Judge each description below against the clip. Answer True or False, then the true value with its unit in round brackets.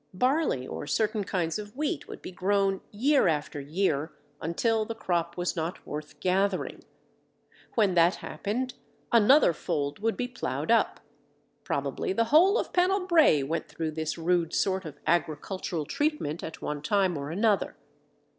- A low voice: False (185 Hz)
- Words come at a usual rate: True (155 wpm)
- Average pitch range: False (6.0 semitones)